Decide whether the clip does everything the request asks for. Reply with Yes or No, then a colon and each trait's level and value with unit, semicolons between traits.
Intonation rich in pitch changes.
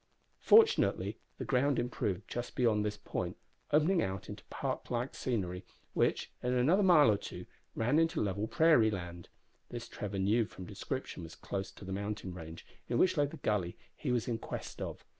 Yes: wide, 6.2 semitones